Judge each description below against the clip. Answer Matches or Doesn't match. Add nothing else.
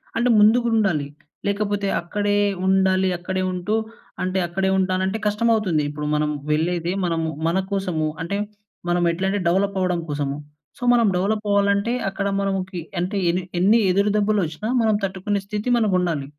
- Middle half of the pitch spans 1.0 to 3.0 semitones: Matches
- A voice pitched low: Doesn't match